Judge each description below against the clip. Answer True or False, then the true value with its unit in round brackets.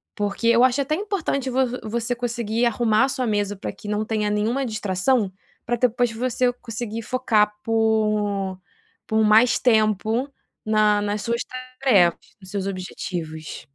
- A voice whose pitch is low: False (220 Hz)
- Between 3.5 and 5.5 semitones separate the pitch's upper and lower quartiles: False (2.8 semitones)